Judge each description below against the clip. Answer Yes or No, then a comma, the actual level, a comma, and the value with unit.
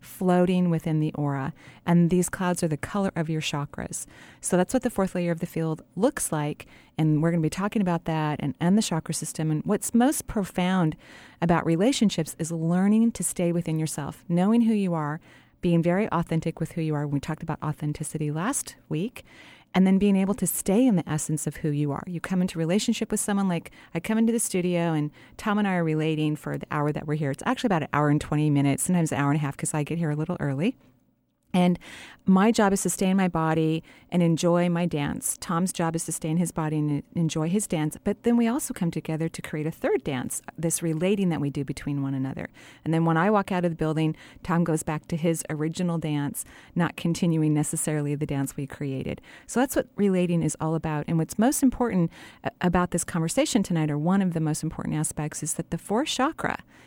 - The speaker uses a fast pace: Yes, fast, 230 wpm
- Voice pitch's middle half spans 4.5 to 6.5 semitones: No, average, 3.4 semitones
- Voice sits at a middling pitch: Yes, medium, 165 Hz